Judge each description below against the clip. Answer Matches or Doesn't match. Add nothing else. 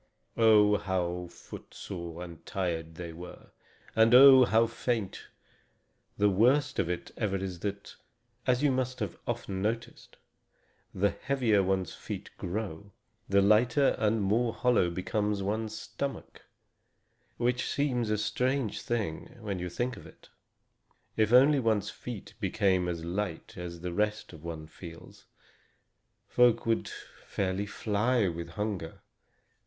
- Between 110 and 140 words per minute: Matches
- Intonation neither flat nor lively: Matches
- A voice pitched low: Matches